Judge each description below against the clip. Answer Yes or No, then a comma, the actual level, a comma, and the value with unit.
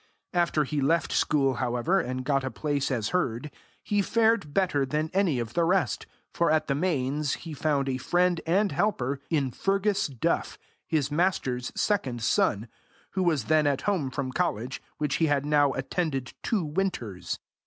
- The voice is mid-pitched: Yes, medium, 150 Hz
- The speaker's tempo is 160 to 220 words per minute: Yes, average, 170 wpm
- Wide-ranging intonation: No, average, 4.9 semitones